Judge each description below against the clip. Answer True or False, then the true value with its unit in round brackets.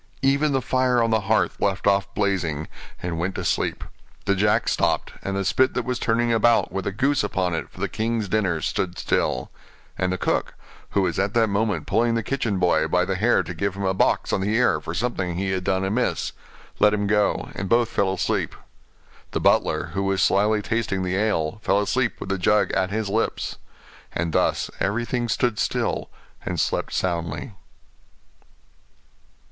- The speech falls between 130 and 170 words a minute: False (190 wpm)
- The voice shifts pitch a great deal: False (3.4 semitones)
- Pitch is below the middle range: True (100 Hz)